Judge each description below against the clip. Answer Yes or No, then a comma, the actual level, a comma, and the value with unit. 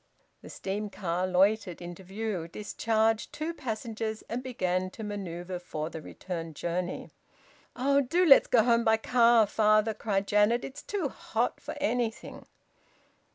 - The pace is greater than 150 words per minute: No, average, 145 wpm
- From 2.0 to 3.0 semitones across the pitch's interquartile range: No, average, 4.1 semitones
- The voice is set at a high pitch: Yes, high, 215 Hz